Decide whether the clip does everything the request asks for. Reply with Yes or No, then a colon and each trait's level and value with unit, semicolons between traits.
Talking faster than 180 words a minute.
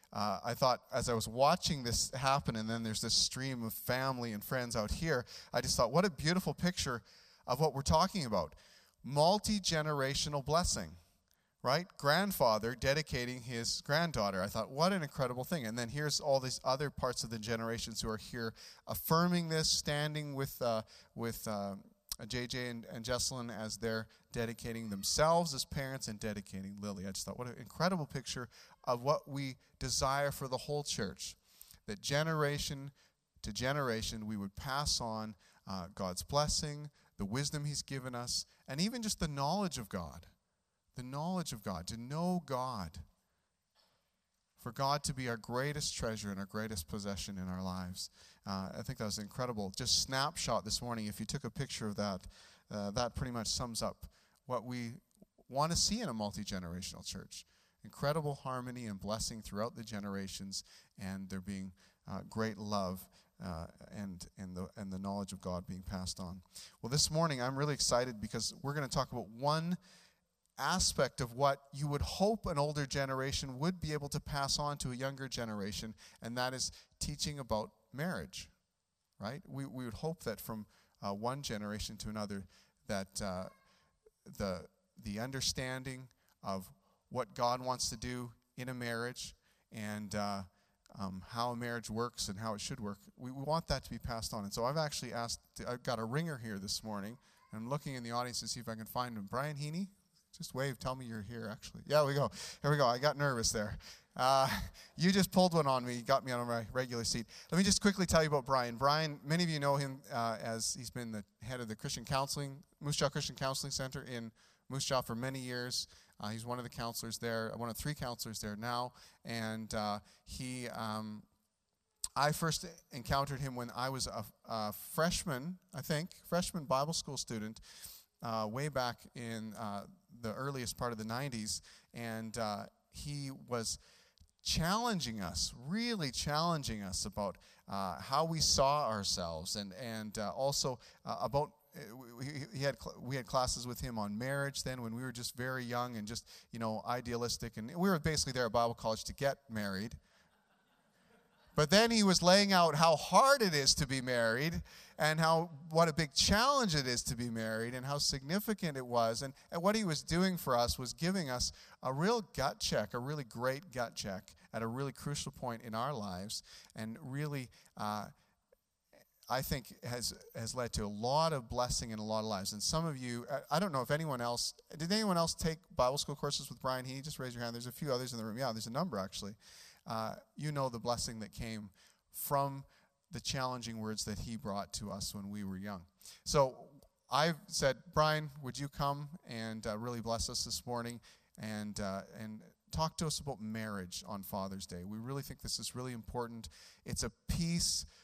Yes: average, 190 wpm